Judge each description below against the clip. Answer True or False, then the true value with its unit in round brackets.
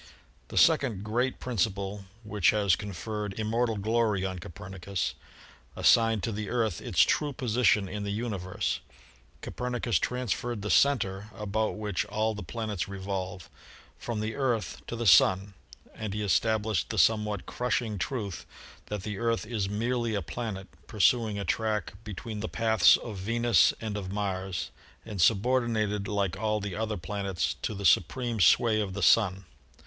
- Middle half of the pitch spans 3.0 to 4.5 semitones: False (2.6 semitones)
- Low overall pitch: True (105 Hz)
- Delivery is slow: False (165 wpm)